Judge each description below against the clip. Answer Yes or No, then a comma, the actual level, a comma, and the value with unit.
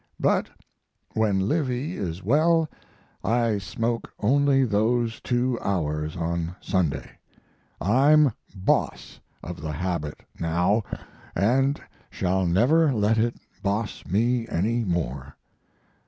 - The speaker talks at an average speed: No, slow, 105 wpm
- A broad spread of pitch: Yes, wide, 5.8 semitones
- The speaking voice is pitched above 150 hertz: No, low, 105 Hz